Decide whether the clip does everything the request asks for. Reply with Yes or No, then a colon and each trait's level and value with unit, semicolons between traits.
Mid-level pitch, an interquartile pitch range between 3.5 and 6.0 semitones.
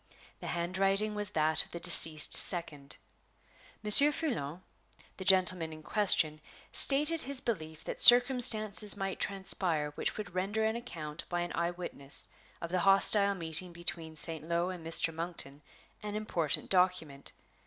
Yes: medium, 180 Hz; average, 4.4 semitones